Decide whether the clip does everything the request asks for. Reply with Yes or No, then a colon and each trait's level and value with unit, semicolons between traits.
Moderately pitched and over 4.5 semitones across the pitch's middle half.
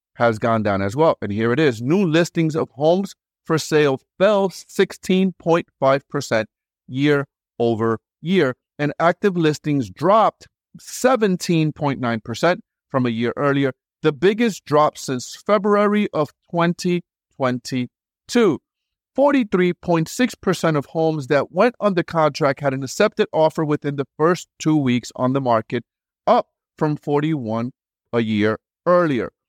Yes: medium, 150 Hz; wide, 5.6 semitones